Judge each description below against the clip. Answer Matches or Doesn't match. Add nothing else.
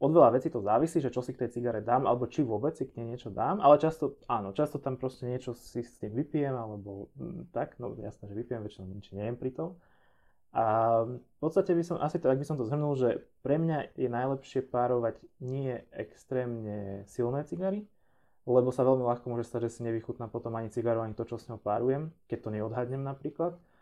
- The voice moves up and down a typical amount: Matches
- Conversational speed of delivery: Doesn't match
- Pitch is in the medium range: Doesn't match